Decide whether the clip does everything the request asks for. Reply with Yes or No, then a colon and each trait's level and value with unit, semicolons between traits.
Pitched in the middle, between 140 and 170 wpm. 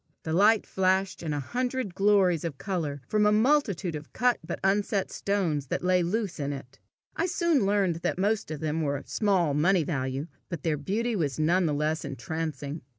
No: medium, 175 Hz; average, 195 wpm